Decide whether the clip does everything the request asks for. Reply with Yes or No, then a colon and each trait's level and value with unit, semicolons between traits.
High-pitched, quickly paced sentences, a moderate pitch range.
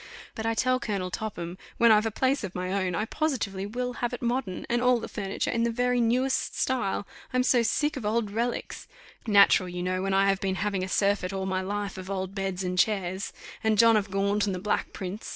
Yes: high, 205 Hz; fast, 230 wpm; average, 3.7 semitones